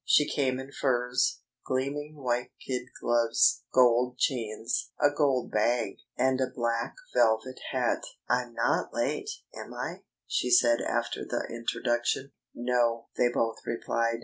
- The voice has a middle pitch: No, low, 125 Hz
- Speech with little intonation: Yes, narrow, 1.8 semitones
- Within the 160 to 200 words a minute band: No, slow, 135 wpm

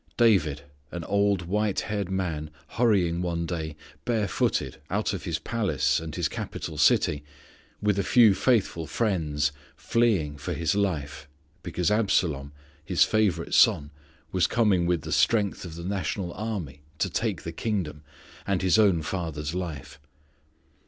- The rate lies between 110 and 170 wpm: Yes, average, 145 wpm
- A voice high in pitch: No, very low, 90 Hz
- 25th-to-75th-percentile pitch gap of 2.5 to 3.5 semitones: No, average, 4.6 semitones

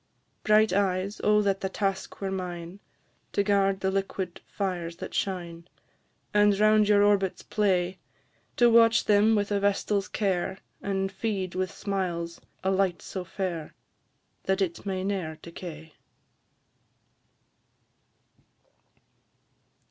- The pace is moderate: No, slow, 120 wpm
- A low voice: No, high, 195 Hz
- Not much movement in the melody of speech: Yes, narrow, 1.9 semitones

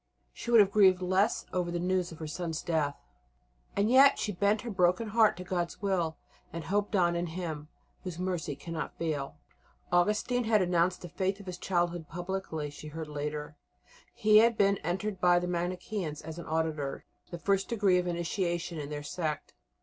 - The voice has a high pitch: No, medium, 175 Hz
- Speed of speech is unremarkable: Yes, average, 185 wpm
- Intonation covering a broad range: No, average, 3.3 semitones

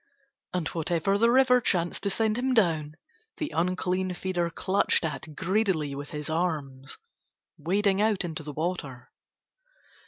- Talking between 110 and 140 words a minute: Yes, slow, 135 wpm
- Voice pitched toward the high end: No, medium, 175 Hz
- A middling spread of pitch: Yes, average, 4.3 semitones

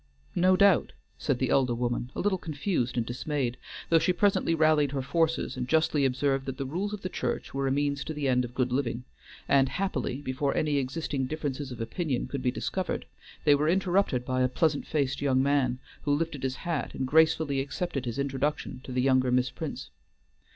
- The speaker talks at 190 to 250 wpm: Yes, average, 200 wpm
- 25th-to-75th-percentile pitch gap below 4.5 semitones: Yes, average, 3.6 semitones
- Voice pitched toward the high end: No, medium, 140 Hz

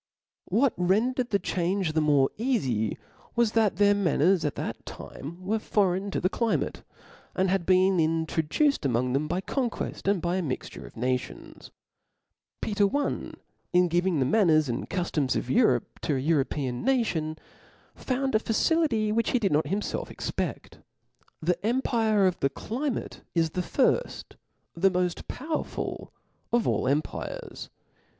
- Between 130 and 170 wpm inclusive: Yes, average, 150 wpm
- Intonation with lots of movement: Yes, wide, 6.1 semitones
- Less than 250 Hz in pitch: Yes, medium, 185 Hz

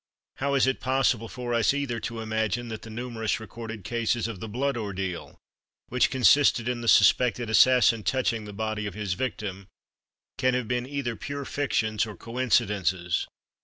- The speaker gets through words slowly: No, average, 165 wpm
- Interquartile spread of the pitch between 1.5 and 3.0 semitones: Yes, average, 2.7 semitones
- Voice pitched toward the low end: Yes, low, 115 Hz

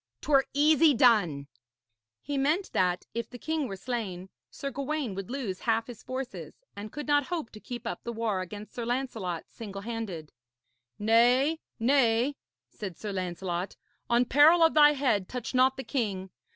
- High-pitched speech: Yes, high, 235 Hz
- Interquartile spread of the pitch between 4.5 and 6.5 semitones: Yes, wide, 5.4 semitones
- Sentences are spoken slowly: No, average, 165 wpm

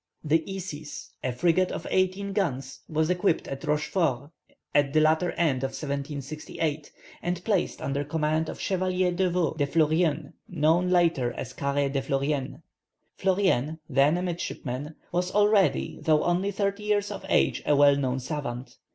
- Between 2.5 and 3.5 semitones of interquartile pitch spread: No, average, 4.3 semitones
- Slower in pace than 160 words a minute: Yes, average, 150 wpm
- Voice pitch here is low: No, medium, 155 Hz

